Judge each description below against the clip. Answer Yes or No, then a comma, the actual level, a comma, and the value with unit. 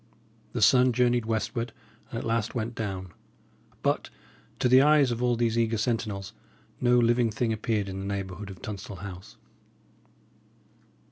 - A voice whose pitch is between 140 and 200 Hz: No, low, 115 Hz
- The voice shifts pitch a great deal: No, average, 3.3 semitones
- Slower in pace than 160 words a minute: Yes, average, 150 wpm